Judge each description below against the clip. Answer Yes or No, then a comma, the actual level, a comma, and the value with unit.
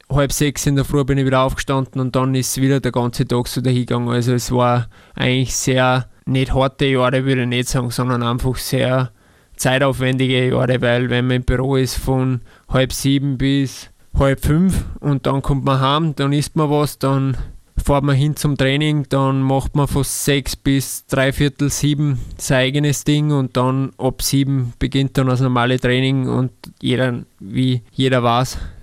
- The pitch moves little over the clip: Yes, narrow, 1.6 semitones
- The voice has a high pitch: No, low, 130 Hz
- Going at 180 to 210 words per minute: Yes, average, 185 wpm